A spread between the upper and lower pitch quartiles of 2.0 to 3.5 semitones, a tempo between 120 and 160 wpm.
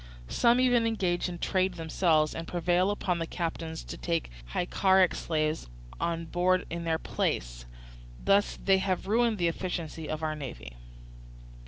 Yes: average, 2.9 semitones; average, 150 wpm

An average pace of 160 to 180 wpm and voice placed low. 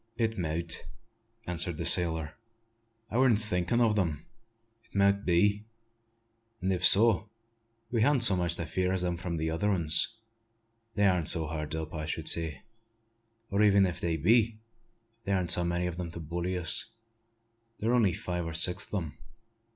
Yes: average, 175 wpm; very low, 90 Hz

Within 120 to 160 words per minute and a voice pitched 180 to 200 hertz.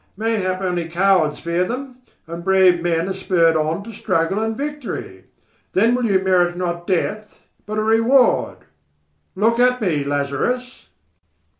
Yes: average, 145 wpm; high, 190 Hz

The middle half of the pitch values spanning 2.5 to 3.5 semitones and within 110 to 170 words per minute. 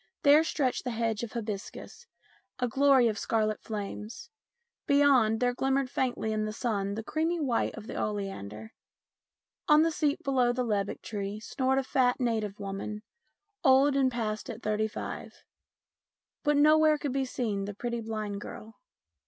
No: average, 4.1 semitones; average, 160 wpm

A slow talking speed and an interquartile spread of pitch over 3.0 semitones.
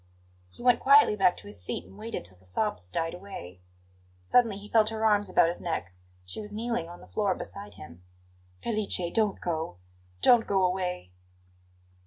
No: average, 180 wpm; average, 5.0 semitones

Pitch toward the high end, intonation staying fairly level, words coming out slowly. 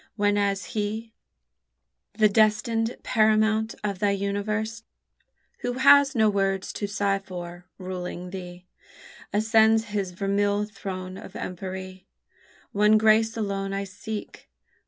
Yes: high, 205 Hz; narrow, 2.2 semitones; slow, 115 wpm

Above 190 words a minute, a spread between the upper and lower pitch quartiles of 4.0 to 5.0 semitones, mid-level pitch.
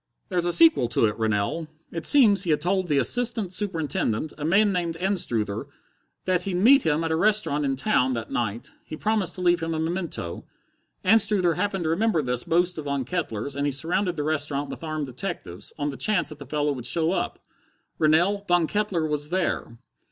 Yes: average, 200 wpm; average, 4.6 semitones; medium, 165 Hz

